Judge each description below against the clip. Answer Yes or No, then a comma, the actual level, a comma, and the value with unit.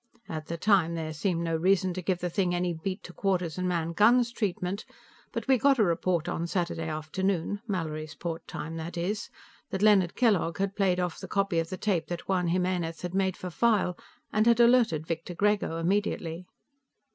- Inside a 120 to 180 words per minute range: No, average, 190 wpm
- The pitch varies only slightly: No, average, 3.1 semitones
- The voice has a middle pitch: Yes, medium, 180 Hz